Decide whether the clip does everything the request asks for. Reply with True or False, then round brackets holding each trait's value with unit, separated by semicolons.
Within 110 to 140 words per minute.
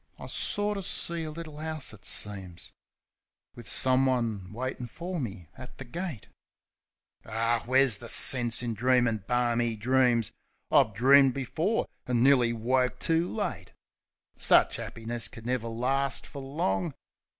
True (135 wpm)